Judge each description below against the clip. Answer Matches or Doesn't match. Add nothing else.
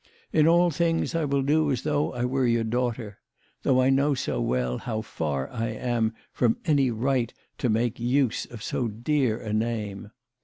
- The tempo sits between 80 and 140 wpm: Doesn't match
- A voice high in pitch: Doesn't match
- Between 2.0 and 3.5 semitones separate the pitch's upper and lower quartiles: Doesn't match